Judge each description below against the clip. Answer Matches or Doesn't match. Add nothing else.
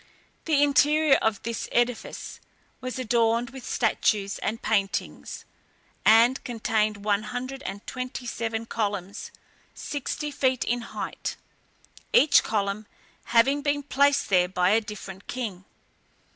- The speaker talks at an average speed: Doesn't match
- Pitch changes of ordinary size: Matches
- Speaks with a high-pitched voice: Matches